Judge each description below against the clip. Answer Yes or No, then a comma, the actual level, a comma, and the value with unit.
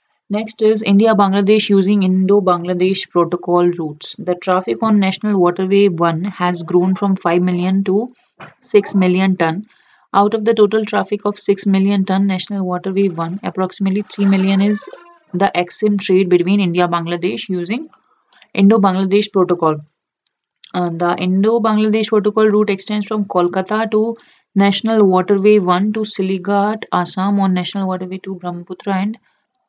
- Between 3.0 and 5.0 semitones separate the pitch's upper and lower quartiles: No, narrow, 2.4 semitones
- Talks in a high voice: Yes, high, 195 Hz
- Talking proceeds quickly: No, average, 145 wpm